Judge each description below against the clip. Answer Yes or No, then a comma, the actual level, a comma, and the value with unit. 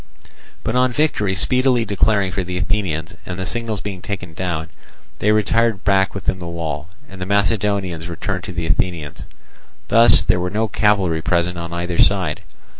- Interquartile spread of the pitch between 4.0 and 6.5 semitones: No, average, 3.4 semitones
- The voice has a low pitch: Yes, very low, 95 Hz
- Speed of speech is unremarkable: Yes, average, 170 wpm